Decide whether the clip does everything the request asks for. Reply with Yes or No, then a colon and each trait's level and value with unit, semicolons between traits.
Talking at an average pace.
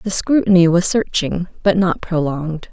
Yes: average, 155 wpm